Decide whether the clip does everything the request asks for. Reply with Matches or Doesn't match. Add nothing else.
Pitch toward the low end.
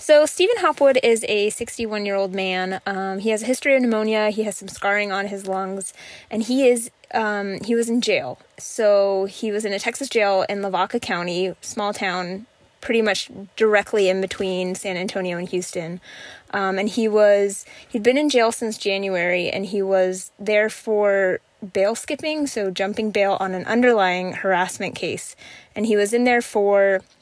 Doesn't match